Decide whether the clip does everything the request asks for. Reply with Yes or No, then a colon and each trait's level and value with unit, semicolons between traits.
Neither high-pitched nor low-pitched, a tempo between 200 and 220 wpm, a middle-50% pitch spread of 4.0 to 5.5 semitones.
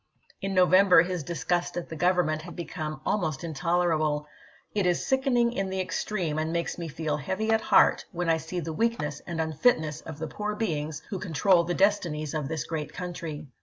No: medium, 170 Hz; fast, 205 wpm; average, 3.2 semitones